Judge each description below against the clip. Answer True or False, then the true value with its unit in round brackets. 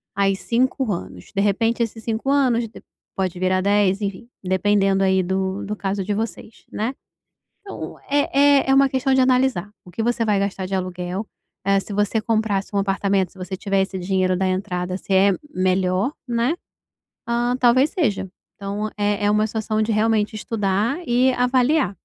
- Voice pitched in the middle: False (205 Hz)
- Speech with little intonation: False (3.6 semitones)